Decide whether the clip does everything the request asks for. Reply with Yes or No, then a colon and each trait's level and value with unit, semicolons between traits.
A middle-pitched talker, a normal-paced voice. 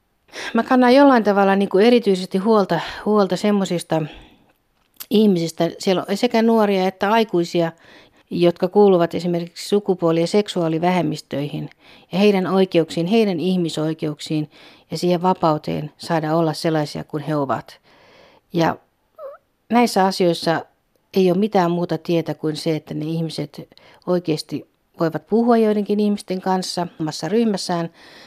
Yes: medium, 180 Hz; average, 125 wpm